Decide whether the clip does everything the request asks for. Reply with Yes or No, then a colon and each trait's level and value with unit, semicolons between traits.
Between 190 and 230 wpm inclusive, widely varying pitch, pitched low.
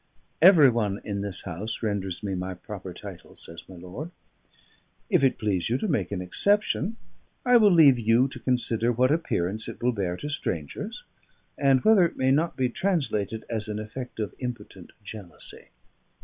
No: average, 175 wpm; wide, 5.9 semitones; low, 115 Hz